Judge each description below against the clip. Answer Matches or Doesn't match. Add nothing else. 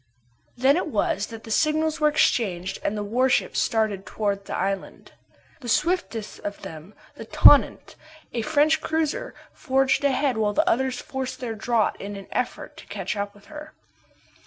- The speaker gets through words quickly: Doesn't match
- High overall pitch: Matches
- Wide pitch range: Matches